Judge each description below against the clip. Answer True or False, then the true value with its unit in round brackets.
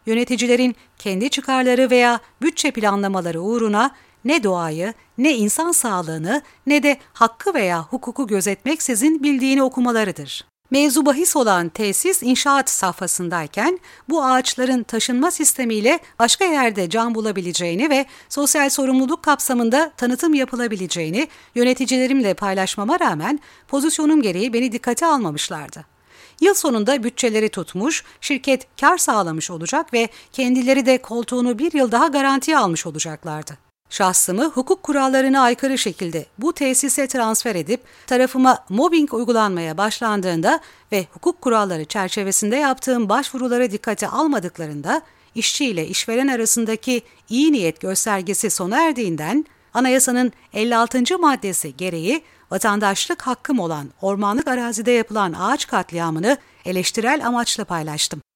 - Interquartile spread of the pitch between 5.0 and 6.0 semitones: True (5.4 semitones)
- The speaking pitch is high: True (245 Hz)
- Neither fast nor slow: True (115 wpm)